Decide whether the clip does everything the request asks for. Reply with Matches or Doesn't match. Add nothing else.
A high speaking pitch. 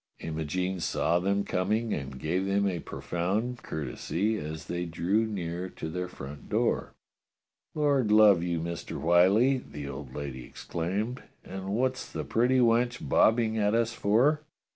Doesn't match